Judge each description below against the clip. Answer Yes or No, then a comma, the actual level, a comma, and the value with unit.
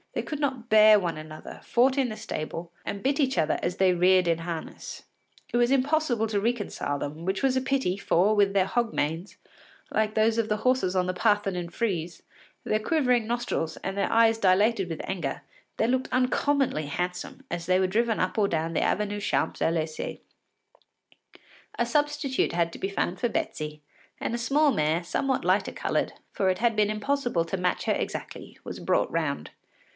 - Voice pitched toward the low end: No, high, 205 Hz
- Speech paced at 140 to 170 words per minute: No, average, 190 wpm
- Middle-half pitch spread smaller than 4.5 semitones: No, wide, 5.5 semitones